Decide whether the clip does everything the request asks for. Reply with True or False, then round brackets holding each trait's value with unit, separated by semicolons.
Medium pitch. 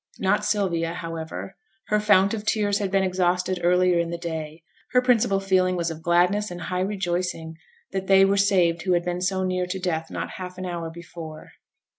True (180 Hz)